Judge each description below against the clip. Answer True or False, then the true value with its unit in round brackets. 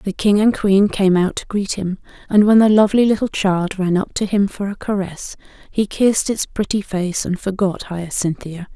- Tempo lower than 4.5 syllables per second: False (5.0 syllables/s)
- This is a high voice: True (195 Hz)